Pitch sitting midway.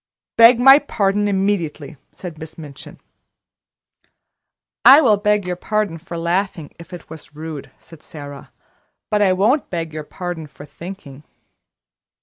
Yes: medium, 175 Hz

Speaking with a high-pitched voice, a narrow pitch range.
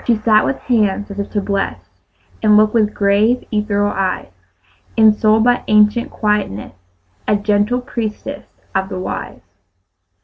Yes: high, 210 Hz; narrow, 1.4 semitones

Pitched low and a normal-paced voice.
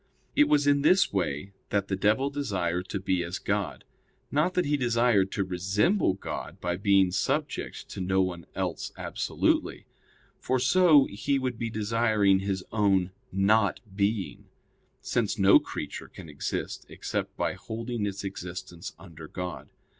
Yes: low, 100 Hz; average, 150 wpm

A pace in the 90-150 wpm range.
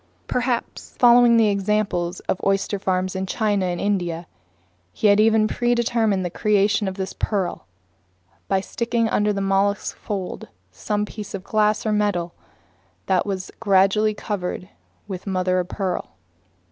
Yes: average, 145 wpm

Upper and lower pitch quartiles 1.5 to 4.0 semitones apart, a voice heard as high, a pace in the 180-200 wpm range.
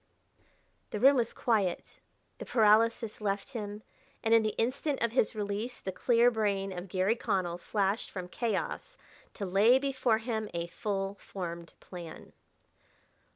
No: average, 3.1 semitones; high, 210 Hz; average, 145 wpm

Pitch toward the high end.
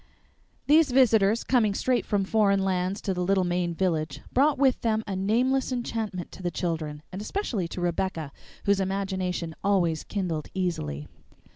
Yes: high, 195 Hz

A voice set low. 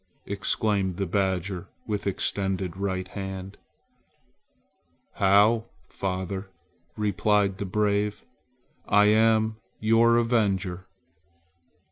Yes: low, 100 Hz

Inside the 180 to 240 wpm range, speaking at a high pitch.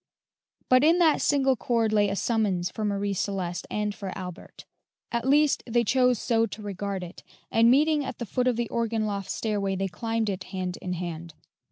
Yes: average, 195 wpm; high, 215 Hz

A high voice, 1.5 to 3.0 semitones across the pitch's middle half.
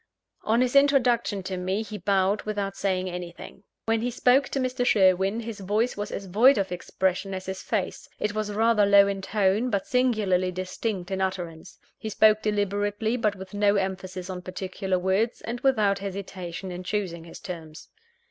Yes: high, 200 Hz; narrow, 2.6 semitones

